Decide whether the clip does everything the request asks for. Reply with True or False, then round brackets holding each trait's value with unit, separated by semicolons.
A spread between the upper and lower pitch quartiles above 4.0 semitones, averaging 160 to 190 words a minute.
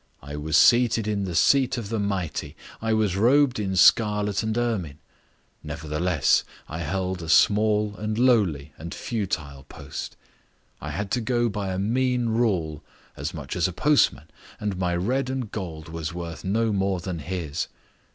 True (5.0 semitones; 165 wpm)